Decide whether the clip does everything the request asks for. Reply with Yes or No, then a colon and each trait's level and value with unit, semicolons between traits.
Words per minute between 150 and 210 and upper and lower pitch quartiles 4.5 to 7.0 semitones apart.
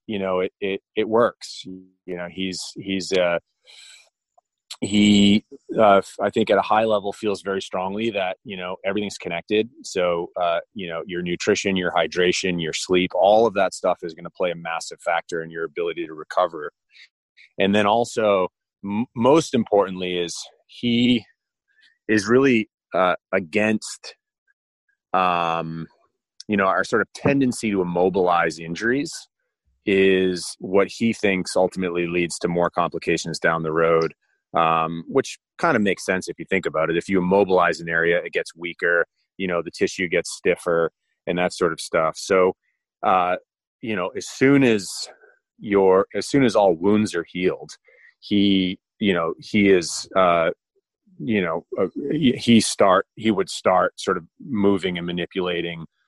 Yes: average, 160 wpm; average, 5.3 semitones